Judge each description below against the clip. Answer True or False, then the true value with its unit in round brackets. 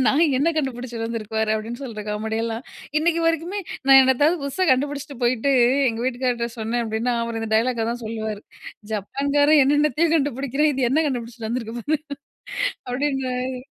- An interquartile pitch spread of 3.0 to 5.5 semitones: True (3.8 semitones)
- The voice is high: True (250 Hz)